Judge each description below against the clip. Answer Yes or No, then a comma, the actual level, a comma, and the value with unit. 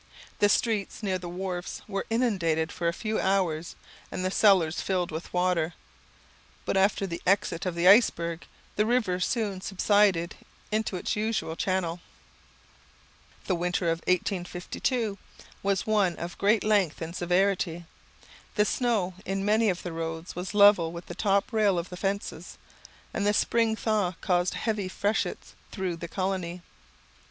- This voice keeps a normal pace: Yes, average, 150 wpm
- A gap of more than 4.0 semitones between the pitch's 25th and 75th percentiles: No, average, 3.0 semitones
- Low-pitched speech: No, medium, 185 Hz